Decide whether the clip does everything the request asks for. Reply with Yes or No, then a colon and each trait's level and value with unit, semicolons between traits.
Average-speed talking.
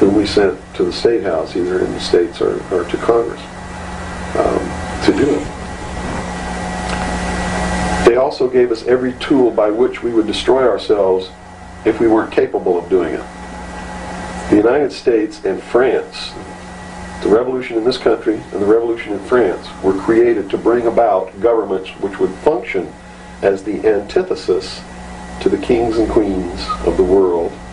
Yes: average, 160 wpm